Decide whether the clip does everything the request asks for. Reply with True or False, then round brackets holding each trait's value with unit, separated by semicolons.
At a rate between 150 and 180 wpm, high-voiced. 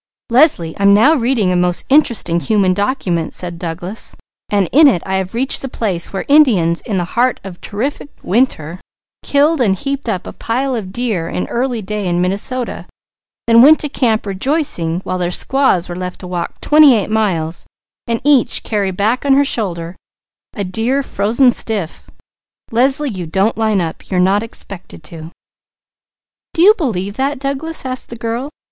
True (175 wpm; 215 Hz)